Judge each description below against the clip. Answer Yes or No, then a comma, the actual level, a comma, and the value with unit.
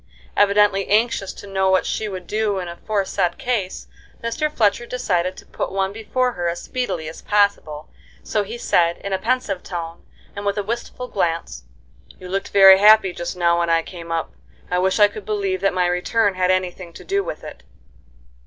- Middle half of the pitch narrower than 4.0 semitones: Yes, average, 3.0 semitones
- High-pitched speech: Yes, high, 195 Hz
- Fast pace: No, average, 195 wpm